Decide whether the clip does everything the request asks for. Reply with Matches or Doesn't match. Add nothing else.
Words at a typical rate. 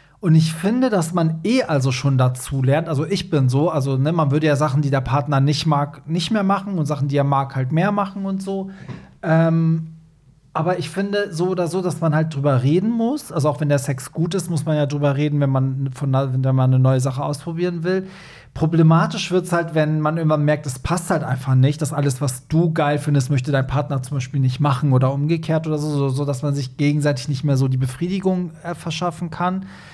Doesn't match